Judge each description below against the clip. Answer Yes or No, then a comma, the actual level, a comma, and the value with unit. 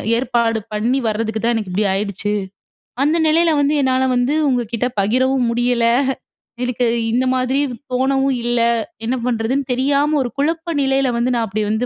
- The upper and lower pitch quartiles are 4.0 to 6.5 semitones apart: No, average, 2.8 semitones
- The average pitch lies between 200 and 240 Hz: No, very high, 250 Hz